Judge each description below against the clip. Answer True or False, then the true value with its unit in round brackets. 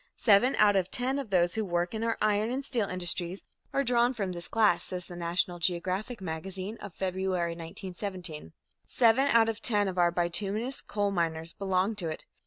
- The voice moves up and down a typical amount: True (4.1 semitones)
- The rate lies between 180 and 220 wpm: True (185 wpm)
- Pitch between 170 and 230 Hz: True (190 Hz)